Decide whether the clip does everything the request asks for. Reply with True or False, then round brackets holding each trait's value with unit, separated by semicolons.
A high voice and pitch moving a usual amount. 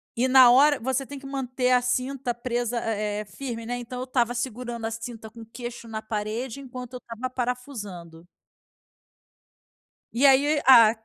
False (245 Hz; 2.3 semitones)